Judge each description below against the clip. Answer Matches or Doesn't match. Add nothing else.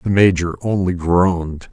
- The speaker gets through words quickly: Doesn't match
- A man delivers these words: Matches